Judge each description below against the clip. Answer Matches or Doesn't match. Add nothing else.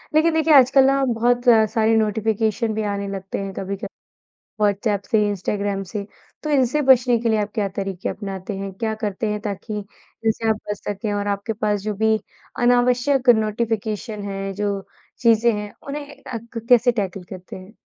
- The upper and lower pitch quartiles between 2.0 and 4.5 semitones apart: Matches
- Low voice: Doesn't match